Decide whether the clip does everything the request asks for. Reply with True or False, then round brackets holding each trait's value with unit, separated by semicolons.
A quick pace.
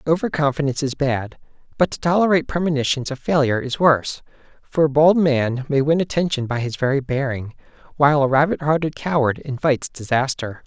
False (170 wpm)